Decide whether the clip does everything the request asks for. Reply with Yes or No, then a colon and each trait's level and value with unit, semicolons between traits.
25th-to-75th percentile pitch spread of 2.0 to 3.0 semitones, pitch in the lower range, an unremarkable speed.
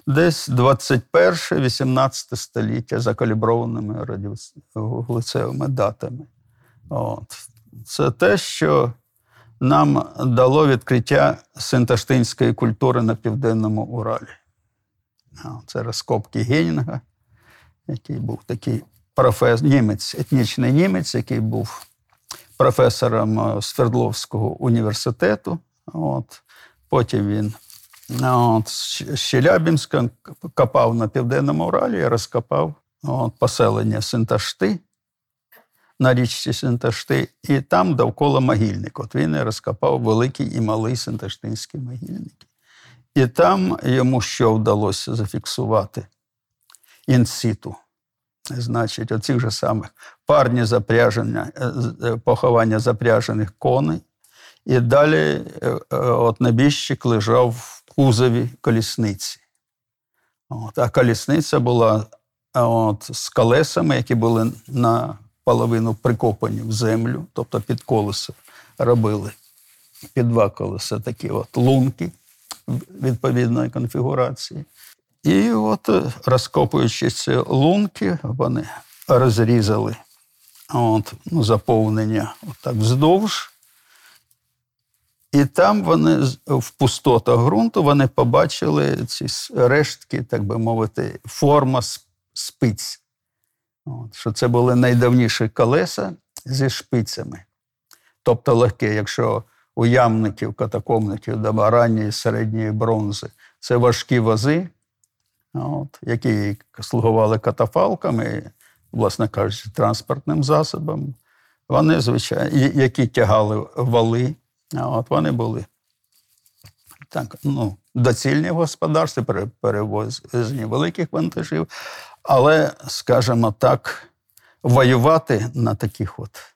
No: average, 2.7 semitones; low, 120 Hz; slow, 90 wpm